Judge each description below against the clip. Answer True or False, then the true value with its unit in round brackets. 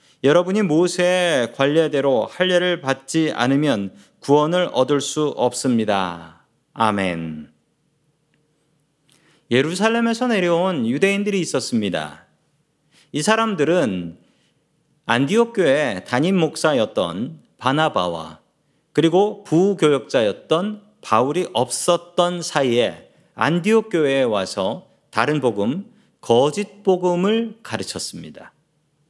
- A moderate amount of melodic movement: True (4.8 semitones)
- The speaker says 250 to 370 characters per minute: False (230 characters per minute)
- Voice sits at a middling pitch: True (155 Hz)